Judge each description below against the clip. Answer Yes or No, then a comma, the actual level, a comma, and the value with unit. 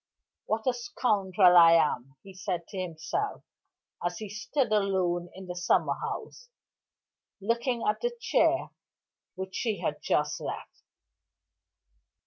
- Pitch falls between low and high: No, high, 195 Hz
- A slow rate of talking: Yes, slow, 125 wpm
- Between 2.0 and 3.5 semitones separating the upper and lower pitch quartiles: No, average, 4.4 semitones